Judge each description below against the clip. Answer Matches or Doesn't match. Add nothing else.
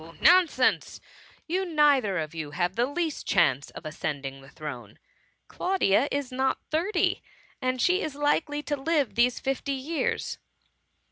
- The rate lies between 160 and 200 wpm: Doesn't match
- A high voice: Matches